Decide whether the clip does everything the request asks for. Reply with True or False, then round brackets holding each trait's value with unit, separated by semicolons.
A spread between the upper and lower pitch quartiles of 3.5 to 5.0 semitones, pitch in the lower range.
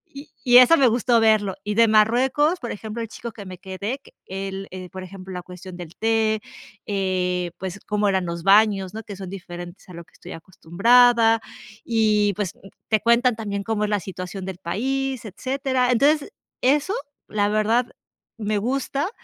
False (4.1 semitones; 210 Hz)